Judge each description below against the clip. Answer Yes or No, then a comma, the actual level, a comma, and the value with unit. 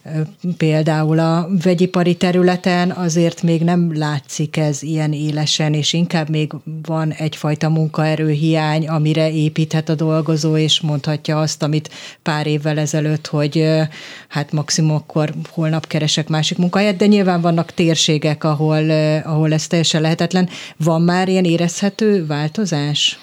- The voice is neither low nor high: Yes, medium, 160 Hz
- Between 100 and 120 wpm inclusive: No, average, 130 wpm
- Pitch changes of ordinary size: No, narrow, 1.8 semitones